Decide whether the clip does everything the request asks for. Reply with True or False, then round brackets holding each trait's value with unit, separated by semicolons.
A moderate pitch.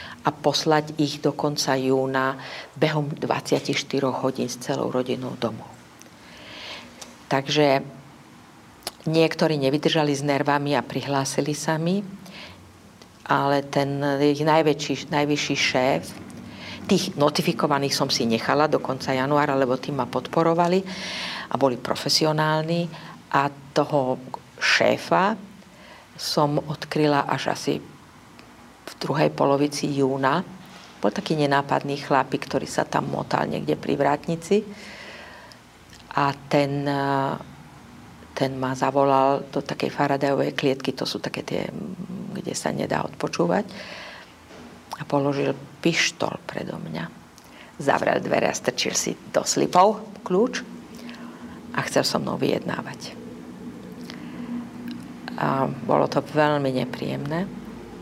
True (145 Hz)